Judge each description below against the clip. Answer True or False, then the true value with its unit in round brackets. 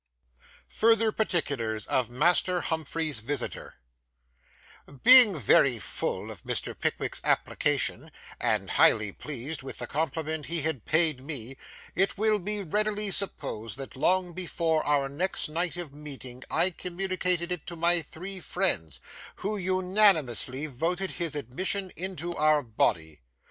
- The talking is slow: True (130 wpm)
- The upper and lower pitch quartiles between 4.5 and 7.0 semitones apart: True (5.3 semitones)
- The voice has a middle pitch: True (165 Hz)